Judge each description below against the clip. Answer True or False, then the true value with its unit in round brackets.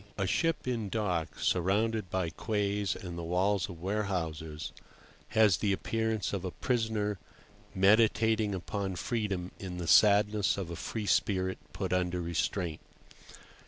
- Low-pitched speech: True (100 Hz)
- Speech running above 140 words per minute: False (135 wpm)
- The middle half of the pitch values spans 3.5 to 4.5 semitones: False (3.0 semitones)